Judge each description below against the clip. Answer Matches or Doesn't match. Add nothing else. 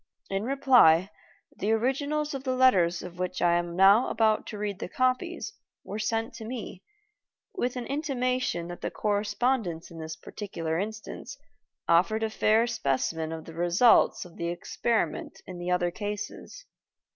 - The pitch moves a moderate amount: Doesn't match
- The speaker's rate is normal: Matches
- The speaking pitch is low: Doesn't match